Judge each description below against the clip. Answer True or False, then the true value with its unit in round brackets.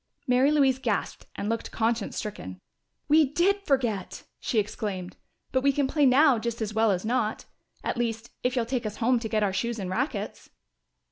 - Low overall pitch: False (235 Hz)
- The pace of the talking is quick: False (190 wpm)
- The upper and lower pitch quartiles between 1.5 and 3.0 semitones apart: False (3.7 semitones)